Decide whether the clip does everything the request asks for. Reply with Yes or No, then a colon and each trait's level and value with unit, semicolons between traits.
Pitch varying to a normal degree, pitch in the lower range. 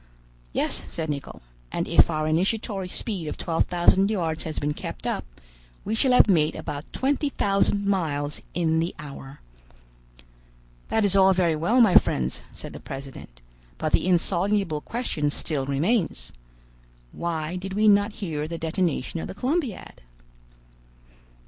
No: average, 4.8 semitones; medium, 170 Hz